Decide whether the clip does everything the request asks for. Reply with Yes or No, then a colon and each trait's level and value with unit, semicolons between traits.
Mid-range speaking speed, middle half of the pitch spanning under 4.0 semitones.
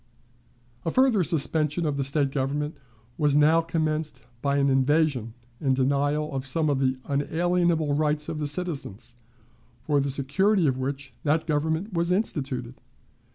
Yes: average, 150 wpm; average, 2.7 semitones